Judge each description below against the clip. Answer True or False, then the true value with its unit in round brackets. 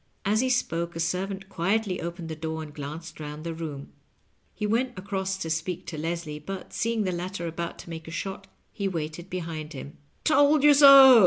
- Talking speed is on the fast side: True (210 wpm)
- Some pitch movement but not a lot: True (3.7 semitones)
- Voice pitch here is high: False (175 Hz)